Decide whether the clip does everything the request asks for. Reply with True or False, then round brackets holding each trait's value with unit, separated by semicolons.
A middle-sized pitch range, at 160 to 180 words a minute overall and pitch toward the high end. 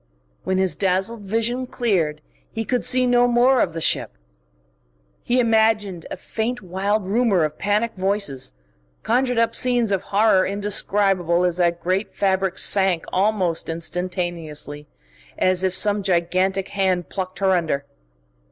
False (3.6 semitones; 140 wpm; 195 Hz)